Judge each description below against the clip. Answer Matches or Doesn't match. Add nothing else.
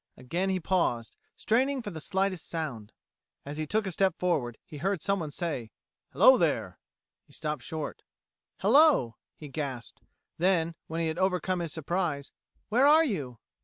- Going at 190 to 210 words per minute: Doesn't match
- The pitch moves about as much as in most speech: Matches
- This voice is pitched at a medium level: Matches